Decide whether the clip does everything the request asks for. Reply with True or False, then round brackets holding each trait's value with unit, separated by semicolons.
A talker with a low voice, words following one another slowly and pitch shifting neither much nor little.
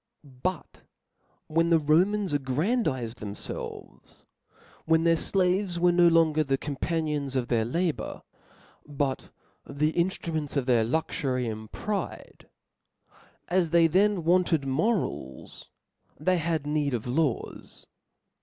False (155 Hz; 115 wpm; 4.4 semitones)